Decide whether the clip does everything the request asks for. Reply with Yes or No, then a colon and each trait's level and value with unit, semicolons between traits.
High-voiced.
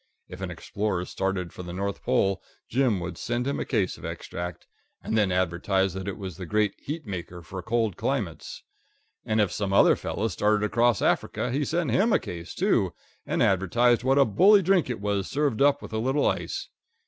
No: low, 105 Hz